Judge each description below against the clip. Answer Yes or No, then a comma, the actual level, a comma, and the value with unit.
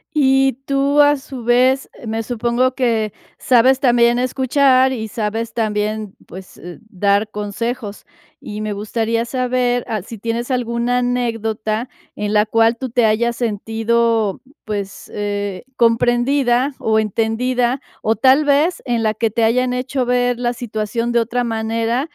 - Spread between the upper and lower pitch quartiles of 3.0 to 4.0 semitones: No, narrow, 2.5 semitones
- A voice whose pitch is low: No, high, 235 Hz